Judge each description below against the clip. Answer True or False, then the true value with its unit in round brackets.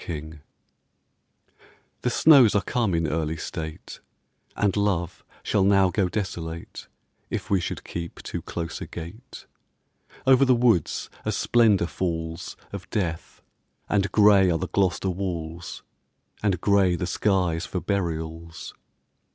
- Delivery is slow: True (130 wpm)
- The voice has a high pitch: False (90 Hz)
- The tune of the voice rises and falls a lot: False (3.5 semitones)